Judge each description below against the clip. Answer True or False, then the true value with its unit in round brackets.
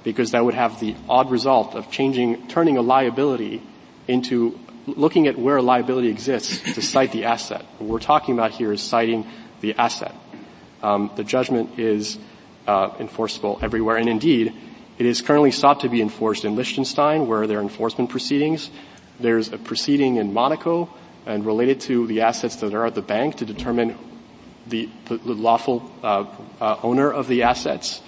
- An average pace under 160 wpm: False (175 wpm)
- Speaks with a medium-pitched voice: False (120 Hz)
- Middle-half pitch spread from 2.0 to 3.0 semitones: True (2.4 semitones)